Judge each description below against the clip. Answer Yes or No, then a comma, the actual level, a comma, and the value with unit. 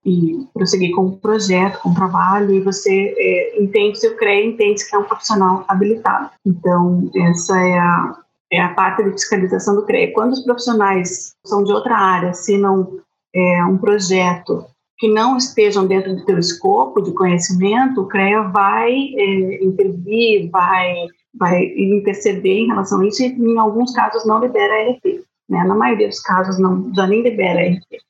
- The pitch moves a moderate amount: Yes, average, 3.0 semitones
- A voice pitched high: Yes, high, 200 Hz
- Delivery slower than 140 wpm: No, average, 180 wpm